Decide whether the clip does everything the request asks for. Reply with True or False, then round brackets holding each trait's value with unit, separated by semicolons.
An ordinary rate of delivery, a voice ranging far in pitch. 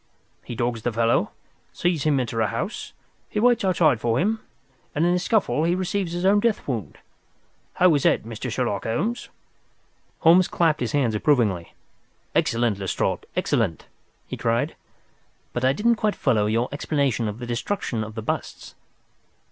True (165 wpm; 7.7 semitones)